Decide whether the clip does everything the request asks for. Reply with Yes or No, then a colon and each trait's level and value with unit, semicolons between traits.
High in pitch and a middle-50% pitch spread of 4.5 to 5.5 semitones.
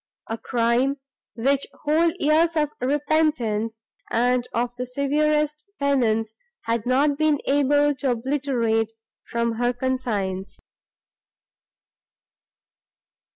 No: very high, 260 Hz; average, 4.0 semitones